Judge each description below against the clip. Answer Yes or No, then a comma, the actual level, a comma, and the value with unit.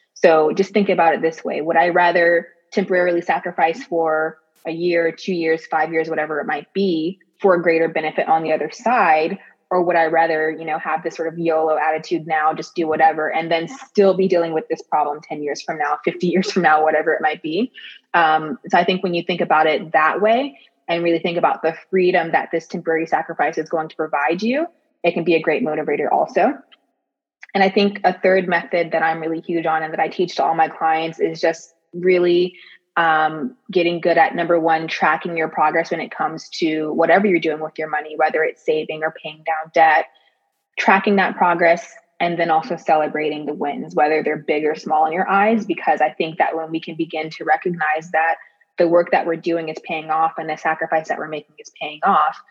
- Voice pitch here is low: No, medium, 165 Hz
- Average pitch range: No, narrow, 2.1 semitones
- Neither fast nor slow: No, fast, 220 wpm